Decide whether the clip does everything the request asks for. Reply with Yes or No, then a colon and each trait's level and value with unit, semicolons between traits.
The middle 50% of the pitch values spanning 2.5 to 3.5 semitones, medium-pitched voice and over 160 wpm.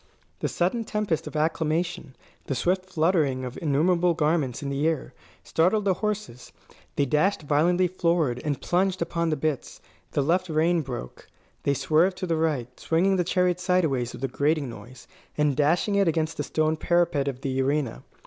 No: average, 4.2 semitones; medium, 160 Hz; average, 175 wpm